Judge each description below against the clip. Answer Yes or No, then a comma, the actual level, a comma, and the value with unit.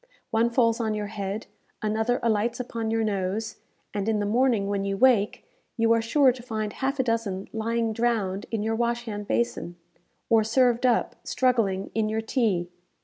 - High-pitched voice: Yes, high, 225 Hz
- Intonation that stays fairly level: Yes, narrow, 2.3 semitones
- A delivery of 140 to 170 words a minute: No, average, 180 wpm